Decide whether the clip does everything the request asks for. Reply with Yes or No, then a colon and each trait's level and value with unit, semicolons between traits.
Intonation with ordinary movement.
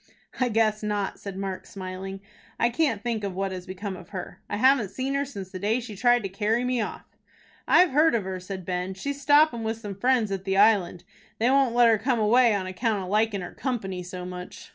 Yes: average, 4.1 semitones